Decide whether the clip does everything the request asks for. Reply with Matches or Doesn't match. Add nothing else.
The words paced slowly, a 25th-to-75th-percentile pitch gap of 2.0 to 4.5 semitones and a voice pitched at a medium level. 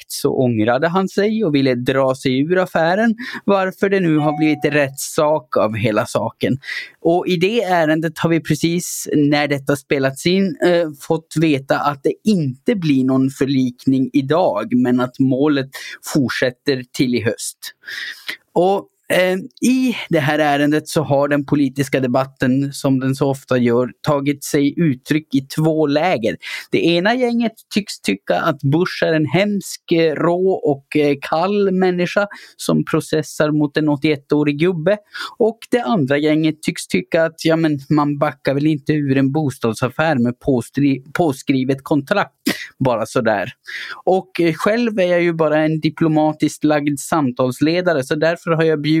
Doesn't match